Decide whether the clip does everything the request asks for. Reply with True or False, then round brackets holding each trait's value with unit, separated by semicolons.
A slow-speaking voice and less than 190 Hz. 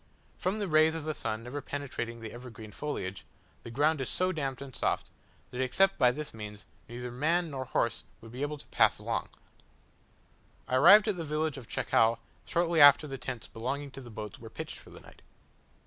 False (200 wpm; 135 Hz)